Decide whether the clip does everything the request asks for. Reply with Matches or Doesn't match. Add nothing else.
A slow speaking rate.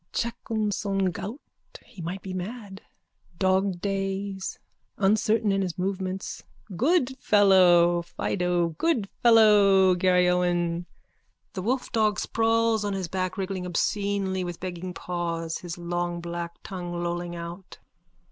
Matches